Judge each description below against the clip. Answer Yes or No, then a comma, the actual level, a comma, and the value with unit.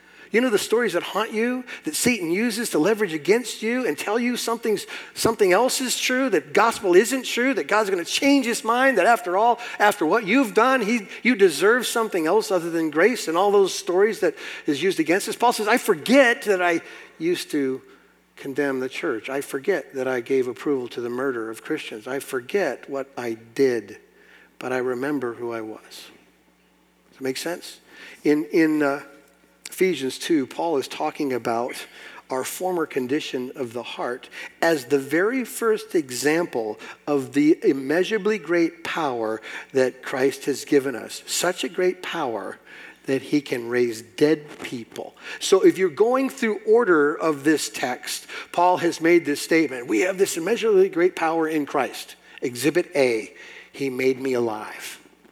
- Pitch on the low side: No, medium, 175 Hz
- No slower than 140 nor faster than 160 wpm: No, average, 175 wpm